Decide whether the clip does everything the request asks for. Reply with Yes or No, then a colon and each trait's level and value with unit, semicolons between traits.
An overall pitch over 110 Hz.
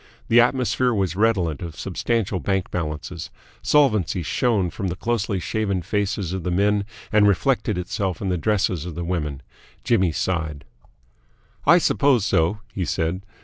No: very low, 95 Hz